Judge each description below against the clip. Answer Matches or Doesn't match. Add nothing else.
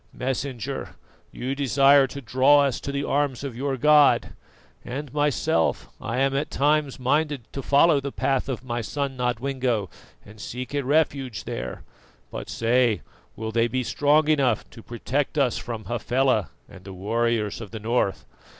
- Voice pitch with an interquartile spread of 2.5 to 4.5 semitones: Matches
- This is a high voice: Doesn't match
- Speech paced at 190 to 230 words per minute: Doesn't match